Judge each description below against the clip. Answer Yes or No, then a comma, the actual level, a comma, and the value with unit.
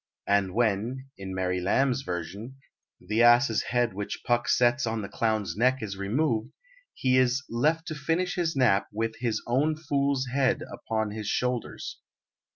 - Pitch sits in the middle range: No, low, 120 Hz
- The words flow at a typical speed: Yes, average, 160 wpm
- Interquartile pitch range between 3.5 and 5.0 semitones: Yes, average, 4.0 semitones